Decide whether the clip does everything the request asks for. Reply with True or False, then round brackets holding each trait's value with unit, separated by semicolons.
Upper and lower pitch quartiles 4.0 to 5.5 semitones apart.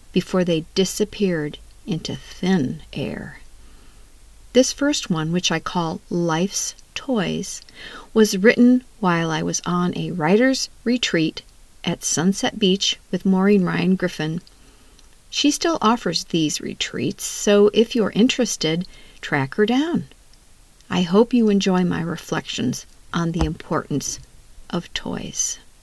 True (4.4 semitones)